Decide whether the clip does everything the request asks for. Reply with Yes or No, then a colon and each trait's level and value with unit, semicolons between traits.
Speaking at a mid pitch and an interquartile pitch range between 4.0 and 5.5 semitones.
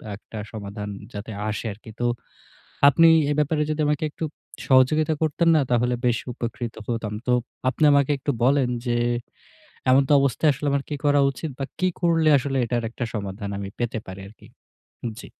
No: low, 130 Hz; average, 4.7 semitones